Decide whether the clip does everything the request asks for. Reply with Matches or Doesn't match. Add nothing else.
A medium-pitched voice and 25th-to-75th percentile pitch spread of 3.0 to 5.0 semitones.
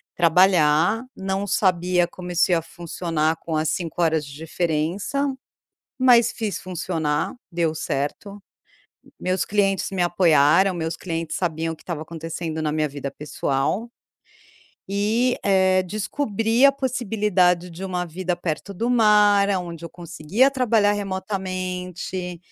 Matches